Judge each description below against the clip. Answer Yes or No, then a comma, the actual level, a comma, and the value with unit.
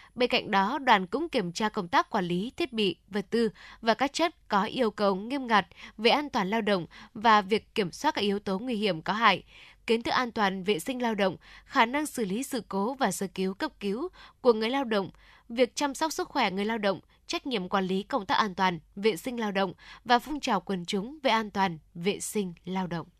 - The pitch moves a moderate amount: Yes, average, 4.5 semitones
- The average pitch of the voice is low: No, high, 220 Hz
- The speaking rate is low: No, average, 245 wpm